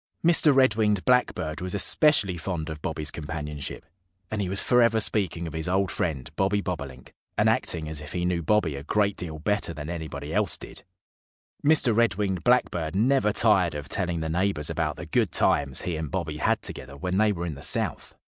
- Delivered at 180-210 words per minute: Yes, average, 200 wpm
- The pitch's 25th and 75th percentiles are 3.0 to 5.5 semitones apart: Yes, average, 5.0 semitones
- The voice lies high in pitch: No, very low, 90 Hz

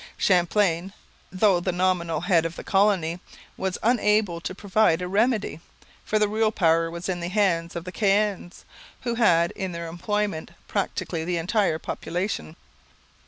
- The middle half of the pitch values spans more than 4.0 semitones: No, average, 3.5 semitones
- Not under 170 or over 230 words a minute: No, average, 155 wpm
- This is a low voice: No, medium, 185 Hz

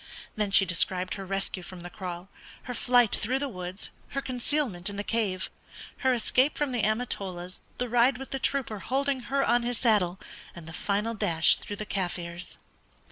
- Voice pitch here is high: Yes, high, 210 Hz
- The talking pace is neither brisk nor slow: Yes, average, 185 wpm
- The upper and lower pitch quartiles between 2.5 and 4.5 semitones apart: No, average, 5.2 semitones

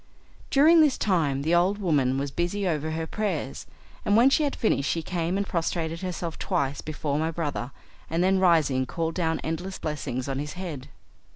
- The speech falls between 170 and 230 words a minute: Yes, average, 185 wpm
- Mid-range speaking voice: Yes, medium, 165 Hz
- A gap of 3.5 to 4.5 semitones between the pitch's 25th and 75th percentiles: Yes, average, 4.2 semitones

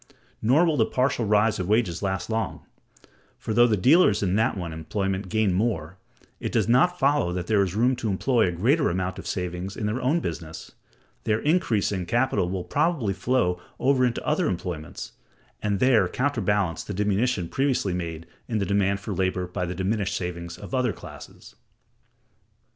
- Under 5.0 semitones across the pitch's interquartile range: No, wide, 5.4 semitones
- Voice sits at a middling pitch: No, low, 100 Hz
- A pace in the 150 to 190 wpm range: Yes, average, 175 wpm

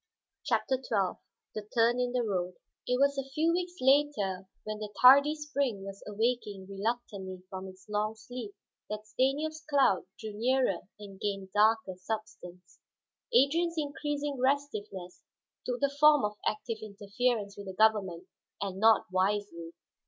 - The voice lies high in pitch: Yes, high, 220 Hz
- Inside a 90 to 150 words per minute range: Yes, average, 145 wpm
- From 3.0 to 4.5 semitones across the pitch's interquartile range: No, wide, 5.4 semitones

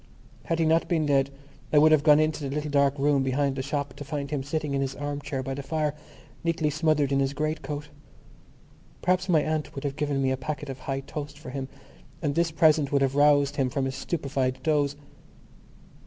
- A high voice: No, medium, 145 Hz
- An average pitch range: No, narrow, 1.9 semitones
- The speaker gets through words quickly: Yes, fast, 220 wpm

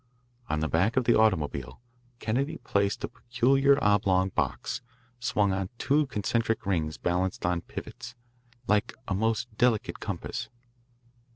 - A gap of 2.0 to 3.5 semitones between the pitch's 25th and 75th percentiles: No, average, 4.4 semitones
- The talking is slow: Yes, slow, 130 wpm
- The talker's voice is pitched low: Yes, low, 105 Hz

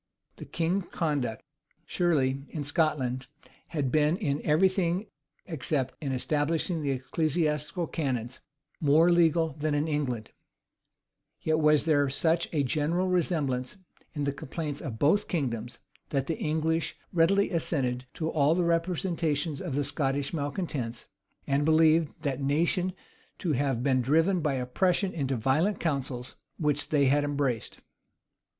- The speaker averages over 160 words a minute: No, average, 140 wpm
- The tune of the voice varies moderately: Yes, average, 3.4 semitones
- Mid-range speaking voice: Yes, medium, 150 Hz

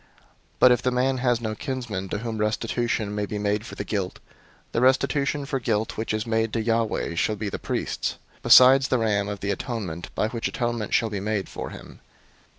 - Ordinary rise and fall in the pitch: Yes, average, 3.0 semitones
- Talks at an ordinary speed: No, fast, 210 wpm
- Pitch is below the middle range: Yes, low, 110 Hz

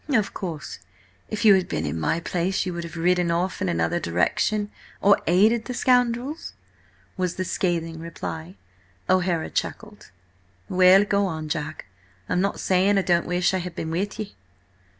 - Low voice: No, medium, 180 Hz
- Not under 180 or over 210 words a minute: No, average, 165 wpm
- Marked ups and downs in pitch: No, average, 3.3 semitones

